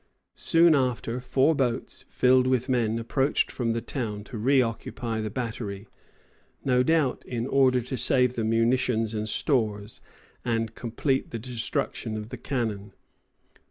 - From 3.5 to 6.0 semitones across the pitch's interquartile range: No, narrow, 2.4 semitones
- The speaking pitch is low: Yes, low, 120 Hz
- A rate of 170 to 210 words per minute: No, average, 145 wpm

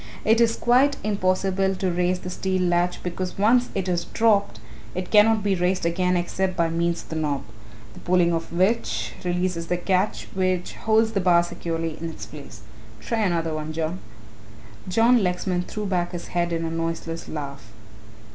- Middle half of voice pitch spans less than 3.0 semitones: Yes, narrow, 2.5 semitones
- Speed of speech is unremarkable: Yes, average, 175 wpm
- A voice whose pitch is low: No, medium, 180 Hz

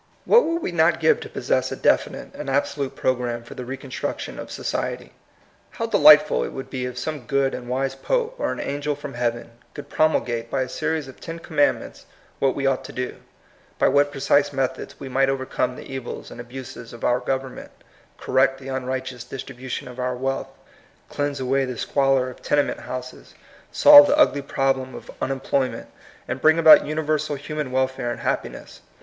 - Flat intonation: Yes, narrow, 2.2 semitones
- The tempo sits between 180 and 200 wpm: Yes, average, 190 wpm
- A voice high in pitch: No, low, 135 Hz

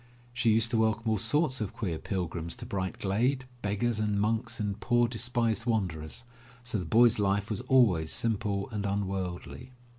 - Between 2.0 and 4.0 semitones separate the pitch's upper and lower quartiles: Yes, average, 3.1 semitones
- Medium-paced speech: Yes, average, 175 wpm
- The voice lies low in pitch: Yes, low, 110 Hz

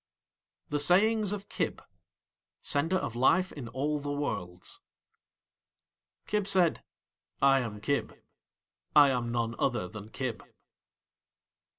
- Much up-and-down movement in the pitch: Yes, wide, 7.0 semitones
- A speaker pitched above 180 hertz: No, medium, 140 Hz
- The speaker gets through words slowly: Yes, slow, 110 wpm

